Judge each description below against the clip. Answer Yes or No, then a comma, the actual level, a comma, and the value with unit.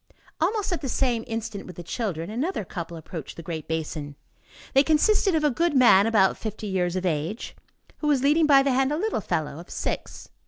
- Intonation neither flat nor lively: No, wide, 9.0 semitones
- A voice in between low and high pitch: No, high, 225 Hz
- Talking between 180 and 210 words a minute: Yes, average, 200 wpm